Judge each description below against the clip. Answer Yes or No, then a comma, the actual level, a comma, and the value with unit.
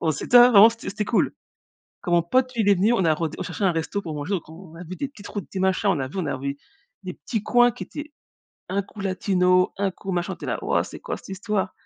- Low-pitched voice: No, high, 190 Hz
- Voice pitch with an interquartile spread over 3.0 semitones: Yes, average, 3.5 semitones